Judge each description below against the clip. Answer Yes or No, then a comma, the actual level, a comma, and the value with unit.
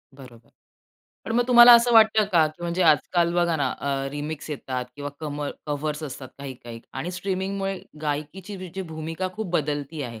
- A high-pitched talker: No, medium, 160 Hz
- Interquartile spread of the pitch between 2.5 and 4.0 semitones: No, average, 4.6 semitones